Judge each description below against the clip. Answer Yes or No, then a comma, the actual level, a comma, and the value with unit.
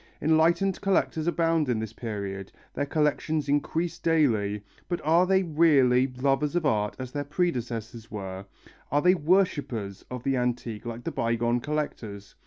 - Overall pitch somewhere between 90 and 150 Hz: Yes, low, 135 Hz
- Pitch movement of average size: No, wide, 5.8 semitones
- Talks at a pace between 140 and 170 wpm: Yes, average, 150 wpm